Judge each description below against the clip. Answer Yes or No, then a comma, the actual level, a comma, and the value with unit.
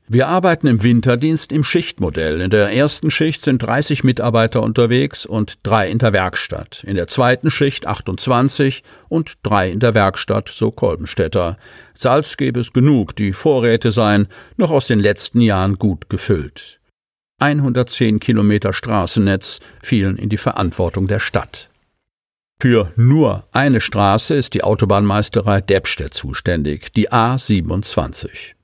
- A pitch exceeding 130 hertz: No, low, 115 Hz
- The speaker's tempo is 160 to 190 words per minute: No, average, 135 wpm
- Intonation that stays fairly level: No, average, 4.4 semitones